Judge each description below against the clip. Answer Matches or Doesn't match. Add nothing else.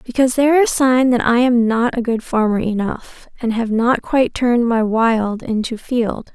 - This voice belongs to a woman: Matches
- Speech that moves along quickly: Matches